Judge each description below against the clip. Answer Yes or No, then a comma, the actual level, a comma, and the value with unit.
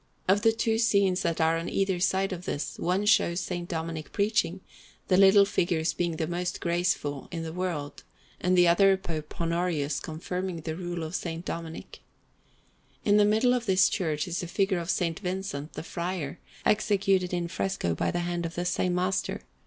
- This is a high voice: No, medium, 175 Hz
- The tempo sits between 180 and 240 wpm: Yes, average, 185 wpm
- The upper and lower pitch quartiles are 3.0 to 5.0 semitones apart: No, narrow, 2.6 semitones